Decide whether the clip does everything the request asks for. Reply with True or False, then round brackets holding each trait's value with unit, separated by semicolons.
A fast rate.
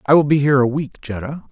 True (275 wpm)